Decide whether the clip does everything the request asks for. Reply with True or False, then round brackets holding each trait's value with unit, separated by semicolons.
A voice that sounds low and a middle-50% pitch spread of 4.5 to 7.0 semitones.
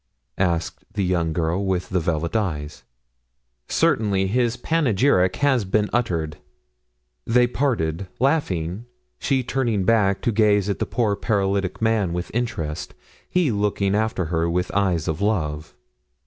True (100 Hz; 4.8 semitones)